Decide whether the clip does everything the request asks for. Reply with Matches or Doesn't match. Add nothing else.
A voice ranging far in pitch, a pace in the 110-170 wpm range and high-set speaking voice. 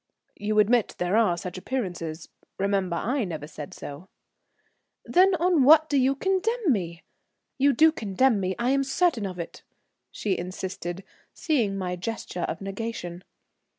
Matches